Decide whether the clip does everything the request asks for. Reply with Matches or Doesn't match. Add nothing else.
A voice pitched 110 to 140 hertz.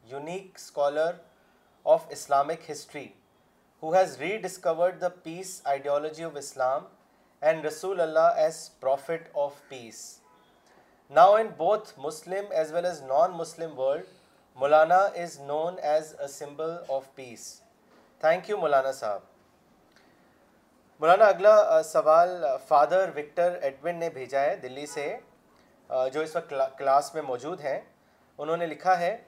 Doesn't match